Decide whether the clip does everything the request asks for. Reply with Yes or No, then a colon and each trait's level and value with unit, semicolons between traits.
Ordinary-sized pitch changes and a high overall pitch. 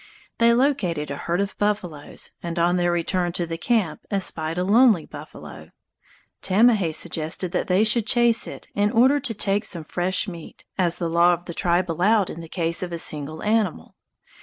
No: average, 3.9 semitones; medium, 180 Hz